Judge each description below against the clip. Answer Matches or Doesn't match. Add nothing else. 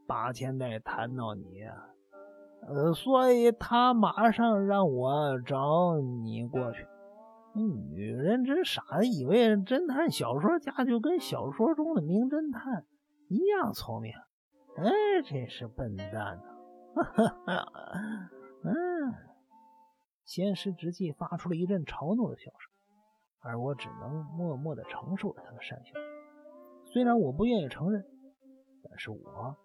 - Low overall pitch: Doesn't match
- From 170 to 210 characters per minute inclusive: Matches